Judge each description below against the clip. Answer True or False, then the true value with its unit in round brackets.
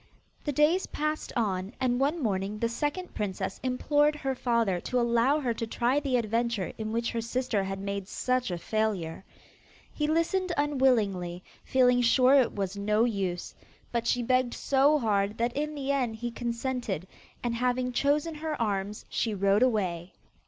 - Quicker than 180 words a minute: False (165 wpm)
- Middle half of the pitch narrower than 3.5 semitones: False (4.6 semitones)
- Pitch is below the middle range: False (235 Hz)